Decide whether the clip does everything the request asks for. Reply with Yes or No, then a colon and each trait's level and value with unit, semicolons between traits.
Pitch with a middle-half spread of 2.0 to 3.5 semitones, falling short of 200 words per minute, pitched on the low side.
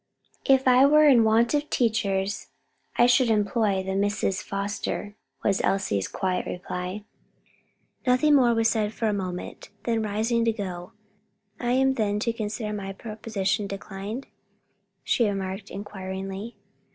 No: average, 3.2 semitones; average, 140 wpm; high, 210 Hz